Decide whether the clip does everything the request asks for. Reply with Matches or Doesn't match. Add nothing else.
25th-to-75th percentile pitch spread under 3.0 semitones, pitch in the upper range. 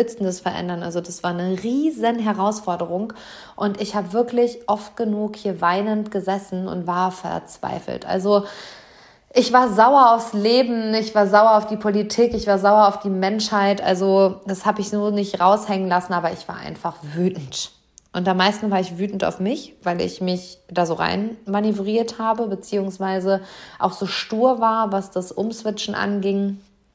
Matches